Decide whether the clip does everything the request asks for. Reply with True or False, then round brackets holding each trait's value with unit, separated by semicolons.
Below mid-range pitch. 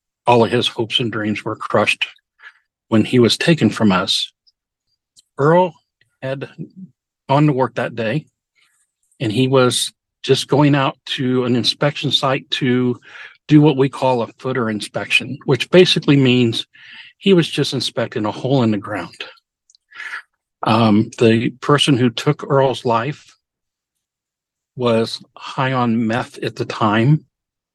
True (125 Hz)